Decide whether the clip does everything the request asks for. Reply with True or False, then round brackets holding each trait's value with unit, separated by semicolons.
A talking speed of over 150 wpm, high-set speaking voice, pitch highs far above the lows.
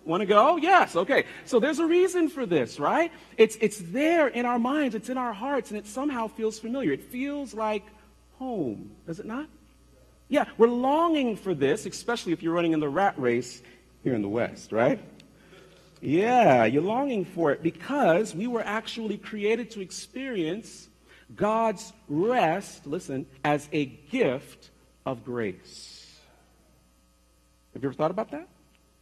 True (160 wpm; 215 Hz; 8.1 semitones)